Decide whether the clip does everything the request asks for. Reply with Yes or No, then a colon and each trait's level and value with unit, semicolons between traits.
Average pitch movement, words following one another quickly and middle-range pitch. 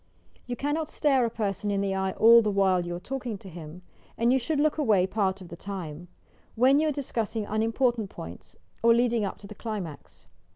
No: average, 4.3 semitones; fast, 215 wpm; high, 215 Hz